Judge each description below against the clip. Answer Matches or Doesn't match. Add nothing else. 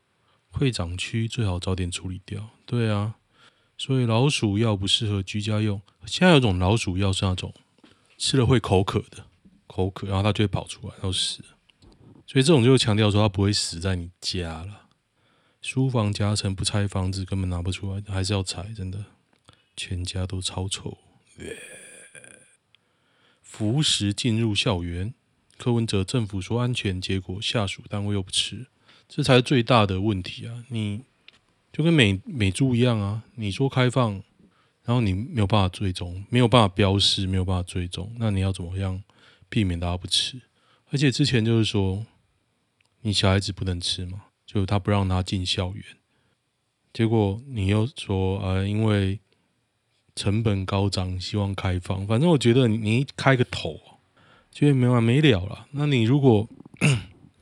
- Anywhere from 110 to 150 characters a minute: Doesn't match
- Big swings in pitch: Doesn't match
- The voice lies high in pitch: Doesn't match